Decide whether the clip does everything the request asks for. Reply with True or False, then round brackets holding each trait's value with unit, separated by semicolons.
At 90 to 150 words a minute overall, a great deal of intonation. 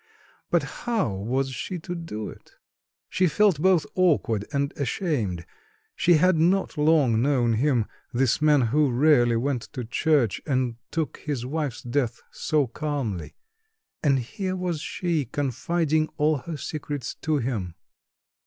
False (140 wpm; 4.8 semitones)